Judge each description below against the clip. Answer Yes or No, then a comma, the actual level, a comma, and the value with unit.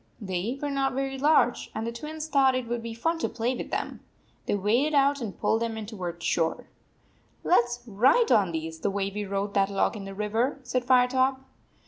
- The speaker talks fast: Yes, fast, 215 wpm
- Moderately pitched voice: No, high, 235 Hz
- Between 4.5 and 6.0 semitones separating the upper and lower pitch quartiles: Yes, average, 4.9 semitones